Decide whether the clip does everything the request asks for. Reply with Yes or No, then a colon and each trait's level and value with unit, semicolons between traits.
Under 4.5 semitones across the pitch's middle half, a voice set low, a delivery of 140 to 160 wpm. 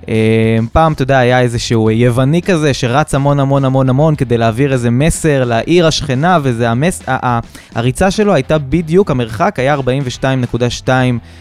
Yes: average, 4.0 semitones; low, 130 Hz; average, 145 wpm